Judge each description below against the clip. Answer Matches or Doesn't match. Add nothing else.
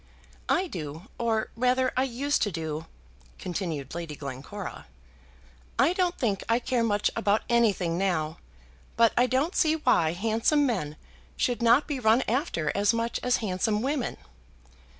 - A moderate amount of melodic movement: Doesn't match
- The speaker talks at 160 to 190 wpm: Doesn't match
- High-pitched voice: Matches